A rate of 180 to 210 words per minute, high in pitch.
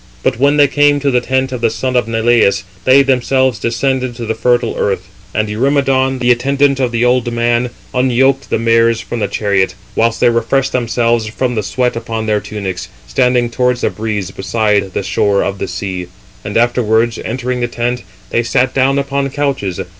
No: average, 190 wpm; low, 120 Hz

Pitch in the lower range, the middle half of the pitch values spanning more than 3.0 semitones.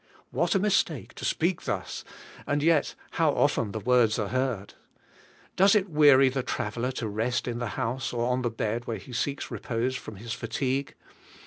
Yes: low, 125 Hz; average, 3.9 semitones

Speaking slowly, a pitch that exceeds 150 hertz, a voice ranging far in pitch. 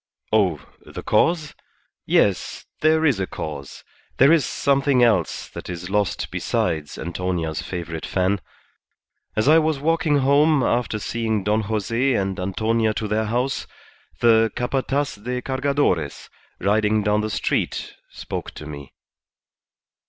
No: slow, 130 wpm; low, 110 Hz; wide, 6.2 semitones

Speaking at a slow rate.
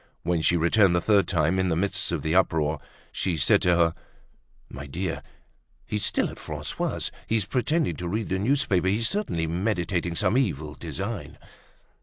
No: average, 170 wpm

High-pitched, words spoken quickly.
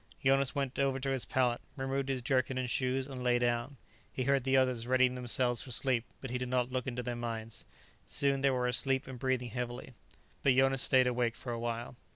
No: low, 130 Hz; fast, 215 wpm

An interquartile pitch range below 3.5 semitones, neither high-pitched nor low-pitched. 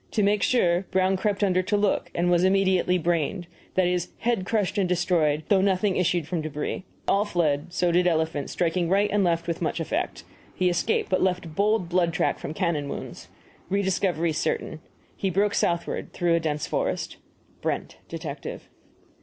Yes: narrow, 2.6 semitones; medium, 180 Hz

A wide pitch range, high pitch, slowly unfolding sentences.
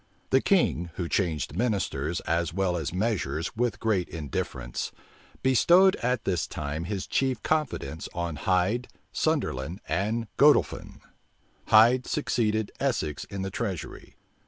No: wide, 6.2 semitones; very low, 95 Hz; slow, 125 wpm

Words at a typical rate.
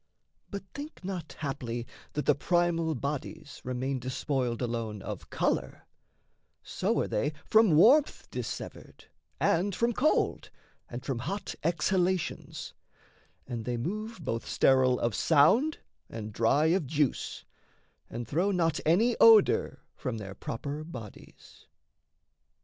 No: slow, 120 wpm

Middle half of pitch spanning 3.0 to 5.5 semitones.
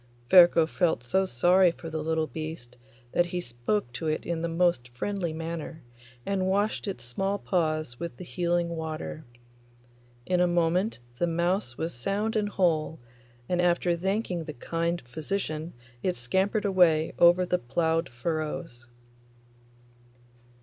No: narrow, 2.6 semitones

